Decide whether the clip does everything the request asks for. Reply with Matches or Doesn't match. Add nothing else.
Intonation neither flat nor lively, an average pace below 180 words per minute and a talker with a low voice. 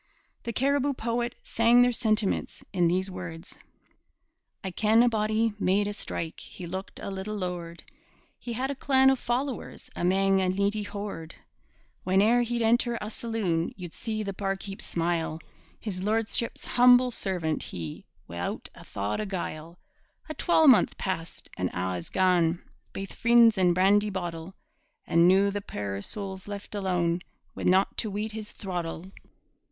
Doesn't match